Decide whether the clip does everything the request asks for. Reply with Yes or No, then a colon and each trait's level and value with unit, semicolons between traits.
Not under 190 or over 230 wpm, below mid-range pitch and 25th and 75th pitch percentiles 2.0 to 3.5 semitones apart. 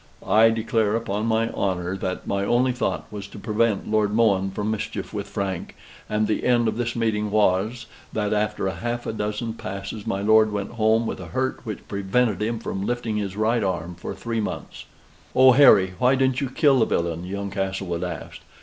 Yes: average, 195 wpm; low, 105 Hz; average, 2.9 semitones